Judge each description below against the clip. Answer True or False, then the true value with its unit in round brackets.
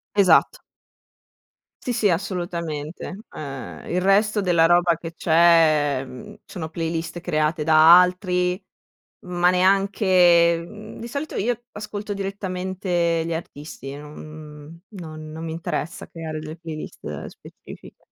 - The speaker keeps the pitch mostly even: False (3.0 semitones)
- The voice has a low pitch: False (170 Hz)